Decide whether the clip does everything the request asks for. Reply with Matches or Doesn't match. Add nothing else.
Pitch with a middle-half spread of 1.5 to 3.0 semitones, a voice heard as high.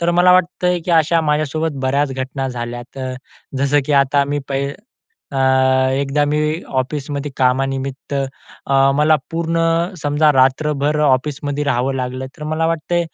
Doesn't match